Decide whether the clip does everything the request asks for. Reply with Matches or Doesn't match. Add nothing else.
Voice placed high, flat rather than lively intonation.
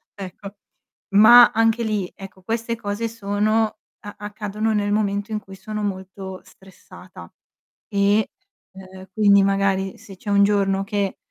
Matches